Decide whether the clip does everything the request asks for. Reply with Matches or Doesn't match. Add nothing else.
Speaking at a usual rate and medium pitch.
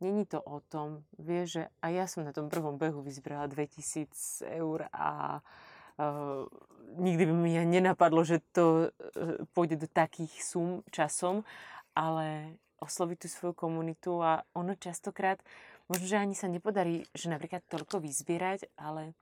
Matches